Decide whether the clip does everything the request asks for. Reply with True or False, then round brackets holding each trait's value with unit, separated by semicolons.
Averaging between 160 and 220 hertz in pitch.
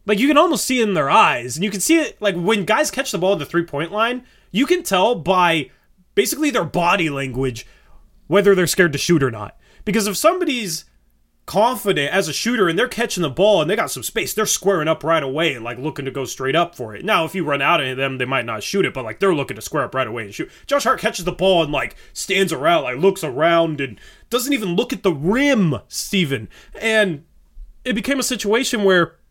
True (190 Hz)